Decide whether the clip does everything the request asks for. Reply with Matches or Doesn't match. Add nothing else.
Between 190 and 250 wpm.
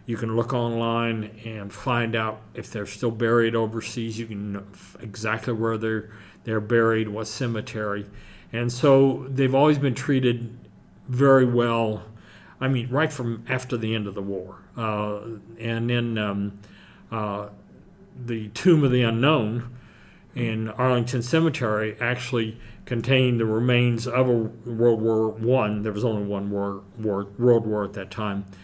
Doesn't match